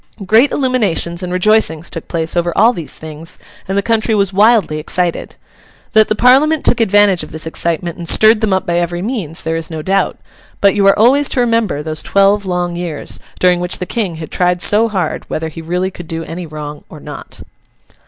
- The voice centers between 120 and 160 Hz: No, medium, 180 Hz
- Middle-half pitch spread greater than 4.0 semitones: Yes, average, 4.6 semitones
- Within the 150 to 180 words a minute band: No, fast, 205 wpm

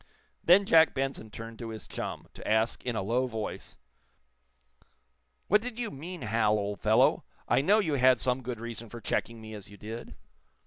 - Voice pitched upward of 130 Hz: No, low, 120 Hz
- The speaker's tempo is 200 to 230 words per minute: No, average, 185 wpm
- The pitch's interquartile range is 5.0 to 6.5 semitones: No, average, 4.1 semitones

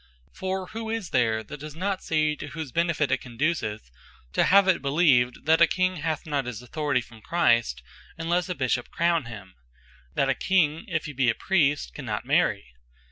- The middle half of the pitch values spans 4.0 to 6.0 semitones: Yes, wide, 5.6 semitones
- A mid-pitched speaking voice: Yes, medium, 150 Hz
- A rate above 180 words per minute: Yes, average, 190 wpm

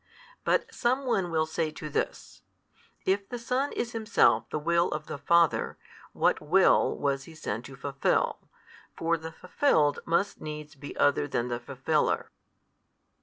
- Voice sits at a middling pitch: Yes, medium, 160 Hz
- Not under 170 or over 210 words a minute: No, average, 155 wpm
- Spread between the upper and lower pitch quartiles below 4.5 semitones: No, average, 4.9 semitones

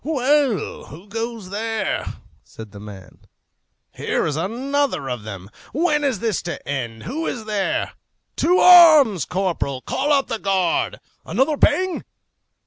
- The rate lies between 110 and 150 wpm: Yes, slow, 135 wpm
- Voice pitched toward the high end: Yes, high, 220 Hz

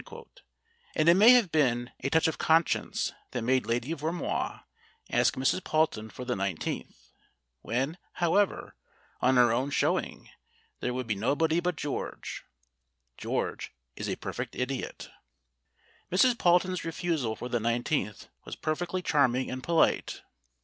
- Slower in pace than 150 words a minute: Yes, average, 140 wpm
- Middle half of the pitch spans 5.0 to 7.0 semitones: Yes, wide, 5.5 semitones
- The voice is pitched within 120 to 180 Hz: Yes, medium, 140 Hz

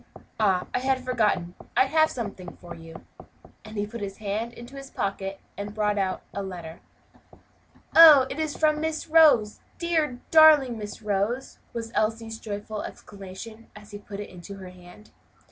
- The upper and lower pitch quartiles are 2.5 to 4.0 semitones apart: No, average, 4.8 semitones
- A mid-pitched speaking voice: No, high, 215 Hz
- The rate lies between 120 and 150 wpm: No, average, 165 wpm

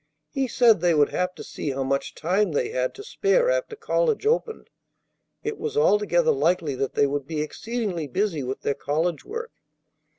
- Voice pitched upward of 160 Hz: Yes, high, 190 Hz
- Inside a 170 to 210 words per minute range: Yes, average, 185 wpm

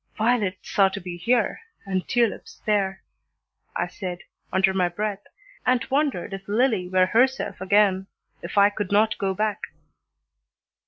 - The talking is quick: No, average, 145 wpm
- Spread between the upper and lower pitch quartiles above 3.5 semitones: No, average, 2.8 semitones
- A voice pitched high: Yes, high, 200 Hz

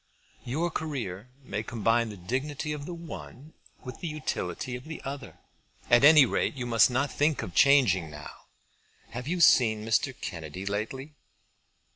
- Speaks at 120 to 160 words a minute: Yes, average, 155 wpm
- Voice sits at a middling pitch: No, low, 125 Hz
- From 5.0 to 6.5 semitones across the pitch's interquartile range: Yes, average, 5.3 semitones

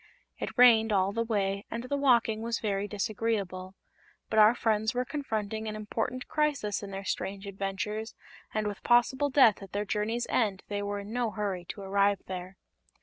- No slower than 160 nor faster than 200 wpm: Yes, average, 180 wpm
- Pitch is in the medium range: No, high, 210 Hz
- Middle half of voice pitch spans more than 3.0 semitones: No, average, 2.7 semitones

